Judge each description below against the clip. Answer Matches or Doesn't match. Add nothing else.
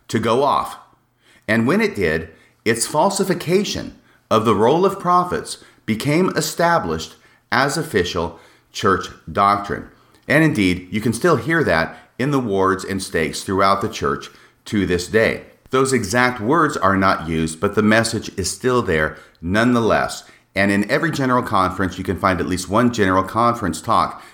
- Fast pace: Doesn't match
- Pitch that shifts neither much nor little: Doesn't match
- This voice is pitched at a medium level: Doesn't match